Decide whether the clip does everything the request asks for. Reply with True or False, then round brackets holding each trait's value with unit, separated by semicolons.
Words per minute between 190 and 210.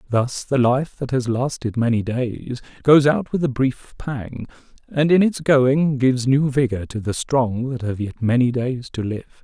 True (195 wpm)